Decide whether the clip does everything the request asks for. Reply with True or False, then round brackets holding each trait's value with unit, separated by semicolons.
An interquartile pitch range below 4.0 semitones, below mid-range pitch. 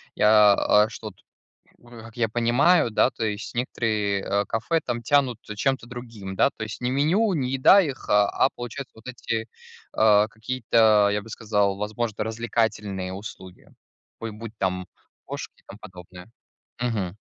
True (2.9 semitones; 110 Hz)